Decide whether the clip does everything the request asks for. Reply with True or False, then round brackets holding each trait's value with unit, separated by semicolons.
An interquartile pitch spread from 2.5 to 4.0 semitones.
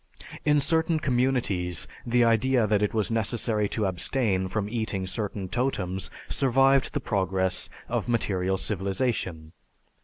False (4.6 semitones)